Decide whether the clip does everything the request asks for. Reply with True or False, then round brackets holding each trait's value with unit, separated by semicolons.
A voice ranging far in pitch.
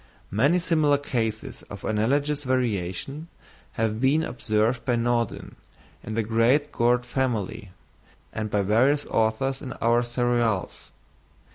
False (3.5 semitones)